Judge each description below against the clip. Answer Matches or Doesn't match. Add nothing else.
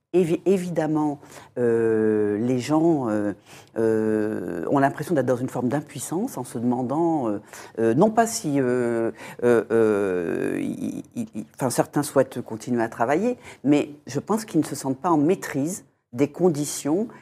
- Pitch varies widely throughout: Matches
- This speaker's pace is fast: Doesn't match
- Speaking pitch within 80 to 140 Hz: Matches